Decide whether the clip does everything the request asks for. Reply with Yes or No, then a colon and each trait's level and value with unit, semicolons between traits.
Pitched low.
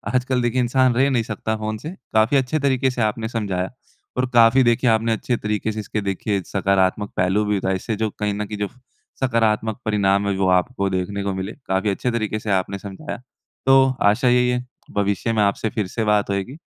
Yes: low, 110 Hz